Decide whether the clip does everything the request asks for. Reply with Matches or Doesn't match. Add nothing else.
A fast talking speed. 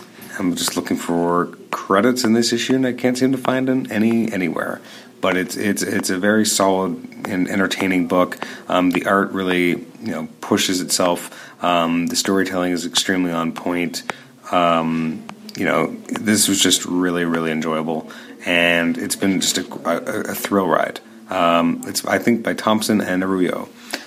Doesn't match